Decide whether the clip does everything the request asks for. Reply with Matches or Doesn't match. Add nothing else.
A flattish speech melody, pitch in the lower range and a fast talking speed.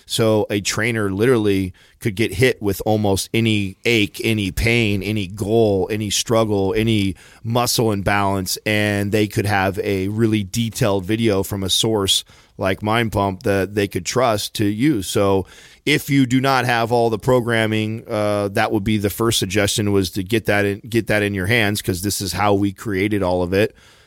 Doesn't match